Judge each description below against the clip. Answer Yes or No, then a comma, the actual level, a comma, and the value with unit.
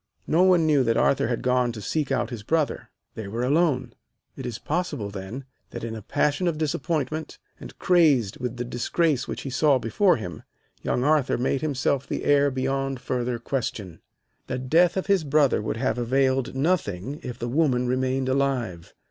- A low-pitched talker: Yes, low, 130 Hz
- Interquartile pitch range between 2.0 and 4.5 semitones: Yes, average, 3.9 semitones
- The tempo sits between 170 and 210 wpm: Yes, average, 180 wpm